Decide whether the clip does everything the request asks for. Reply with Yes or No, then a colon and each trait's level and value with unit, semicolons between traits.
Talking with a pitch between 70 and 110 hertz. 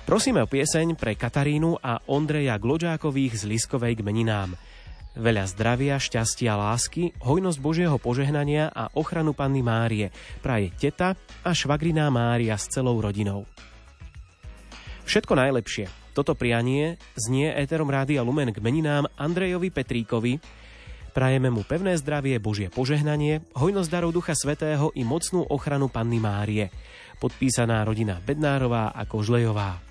No: low, 130 Hz